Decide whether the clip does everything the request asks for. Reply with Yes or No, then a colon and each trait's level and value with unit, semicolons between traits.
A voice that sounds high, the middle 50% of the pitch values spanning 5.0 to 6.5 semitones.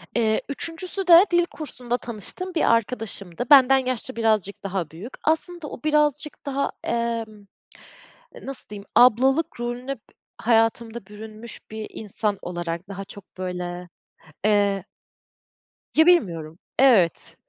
Yes: high, 230 Hz; average, 5.3 semitones